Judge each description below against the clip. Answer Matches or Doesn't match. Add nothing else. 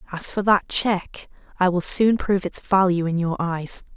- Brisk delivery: Doesn't match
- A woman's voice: Matches